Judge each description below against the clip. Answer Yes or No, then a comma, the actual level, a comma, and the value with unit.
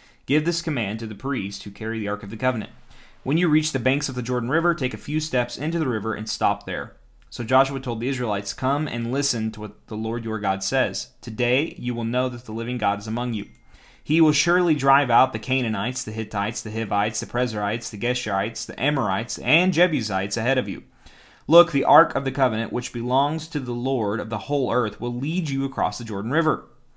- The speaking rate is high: Yes, fast, 225 wpm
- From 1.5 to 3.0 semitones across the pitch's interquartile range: No, average, 3.7 semitones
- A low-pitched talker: Yes, low, 120 Hz